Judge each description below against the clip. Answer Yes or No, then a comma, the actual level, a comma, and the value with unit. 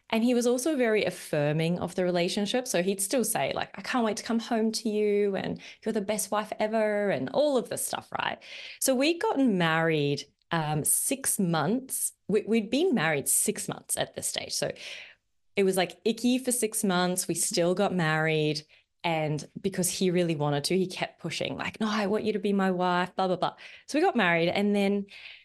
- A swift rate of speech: Yes, fast, 210 wpm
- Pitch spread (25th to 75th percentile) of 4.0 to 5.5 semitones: Yes, average, 4.4 semitones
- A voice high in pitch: Yes, high, 200 Hz